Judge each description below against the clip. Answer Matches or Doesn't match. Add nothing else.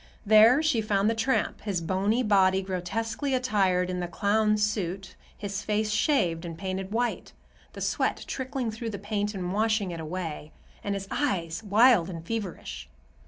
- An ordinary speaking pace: Matches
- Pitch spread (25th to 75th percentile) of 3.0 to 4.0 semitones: Matches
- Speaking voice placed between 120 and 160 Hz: Doesn't match